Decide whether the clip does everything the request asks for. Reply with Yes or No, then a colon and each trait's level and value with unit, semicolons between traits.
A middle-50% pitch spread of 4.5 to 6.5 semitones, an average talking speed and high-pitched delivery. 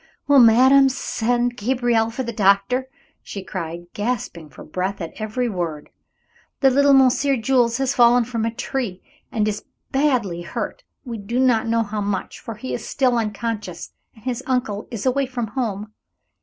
No: average, 3.8 semitones; average, 170 wpm; high, 230 Hz